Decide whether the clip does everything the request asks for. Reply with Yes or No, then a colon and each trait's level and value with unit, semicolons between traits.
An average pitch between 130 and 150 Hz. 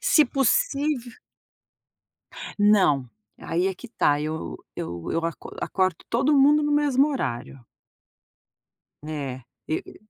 No: high, 190 Hz